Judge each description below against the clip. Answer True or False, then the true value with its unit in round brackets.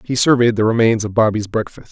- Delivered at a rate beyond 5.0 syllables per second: True (6.2 syllables/s)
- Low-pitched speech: True (115 Hz)